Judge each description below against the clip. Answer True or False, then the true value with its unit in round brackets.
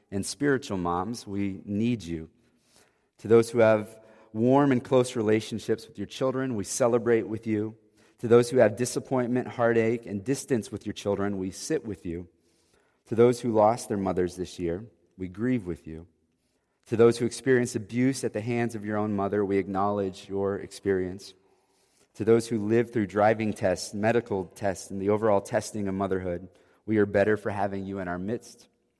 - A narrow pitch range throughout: False (3.2 semitones)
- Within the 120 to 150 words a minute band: False (180 wpm)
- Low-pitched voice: True (105 Hz)